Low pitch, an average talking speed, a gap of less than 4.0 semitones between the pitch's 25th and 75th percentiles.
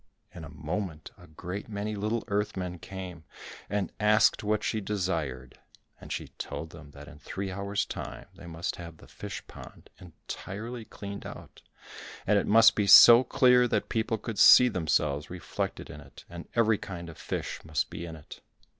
No: very low, 95 Hz; average, 180 wpm; average, 4.6 semitones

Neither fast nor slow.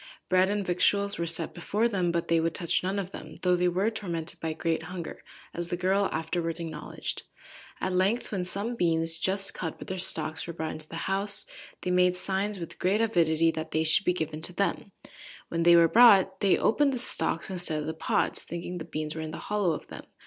No: fast, 220 wpm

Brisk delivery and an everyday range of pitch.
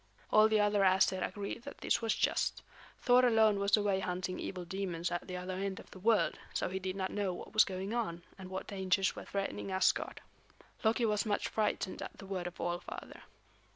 No: fast, 210 wpm; narrow, 2.3 semitones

